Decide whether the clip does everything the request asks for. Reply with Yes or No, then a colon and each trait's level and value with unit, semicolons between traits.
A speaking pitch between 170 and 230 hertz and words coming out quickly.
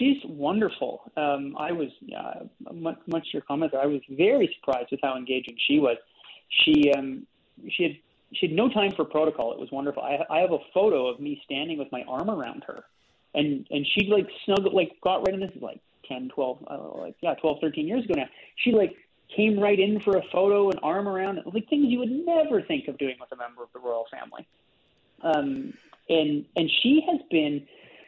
Yes: high, 190 Hz; fast, 215 wpm